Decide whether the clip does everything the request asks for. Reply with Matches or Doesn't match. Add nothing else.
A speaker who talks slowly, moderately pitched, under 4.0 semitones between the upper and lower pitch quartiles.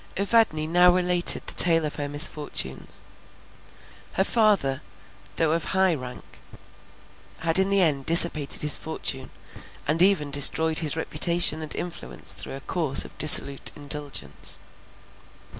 Matches